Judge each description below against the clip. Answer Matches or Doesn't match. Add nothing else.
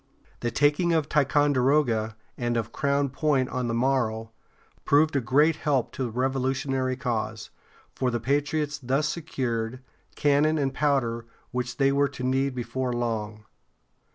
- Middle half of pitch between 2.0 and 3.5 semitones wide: Matches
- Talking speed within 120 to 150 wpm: Matches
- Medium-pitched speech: Doesn't match